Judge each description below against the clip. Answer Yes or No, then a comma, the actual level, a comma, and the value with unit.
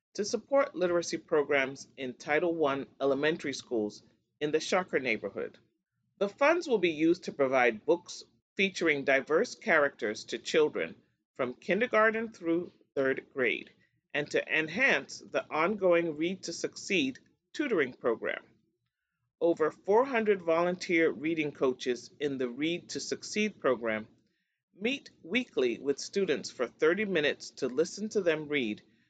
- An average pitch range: No, wide, 7.5 semitones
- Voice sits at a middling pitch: Yes, medium, 170 Hz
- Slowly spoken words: Yes, slow, 130 wpm